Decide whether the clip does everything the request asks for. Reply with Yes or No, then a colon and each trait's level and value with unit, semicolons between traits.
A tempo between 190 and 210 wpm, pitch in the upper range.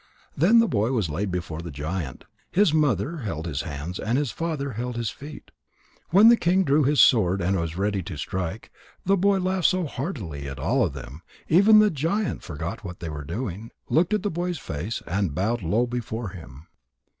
No: average, 200 wpm; low, 110 Hz